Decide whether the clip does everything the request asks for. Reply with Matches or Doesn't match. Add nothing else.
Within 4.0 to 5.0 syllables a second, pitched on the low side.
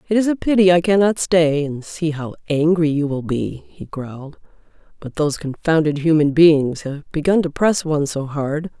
Doesn't match